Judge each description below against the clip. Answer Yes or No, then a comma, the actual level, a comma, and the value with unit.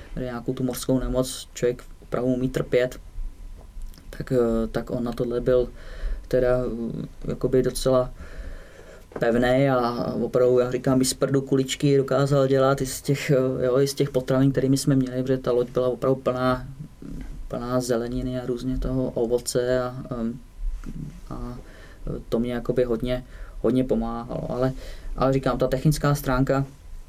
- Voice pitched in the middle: No, low, 125 Hz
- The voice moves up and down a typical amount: No, narrow, 1.5 semitones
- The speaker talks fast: No, average, 140 wpm